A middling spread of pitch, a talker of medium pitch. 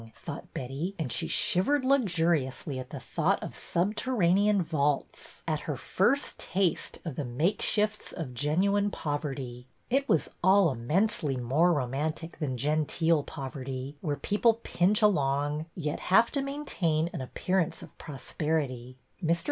No: wide, 5.8 semitones; medium, 160 Hz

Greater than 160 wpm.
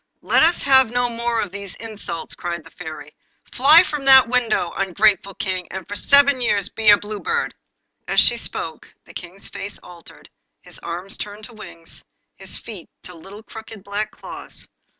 Yes: average, 175 wpm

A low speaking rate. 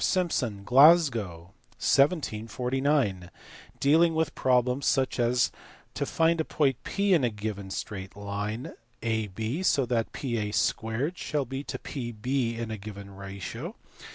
Yes: slow, 130 wpm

